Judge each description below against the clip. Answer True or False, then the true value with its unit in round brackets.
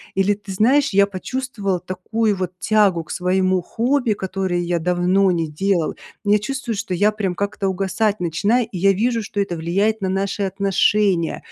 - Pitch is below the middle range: False (195 Hz)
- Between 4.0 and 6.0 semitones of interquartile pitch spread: False (2.6 semitones)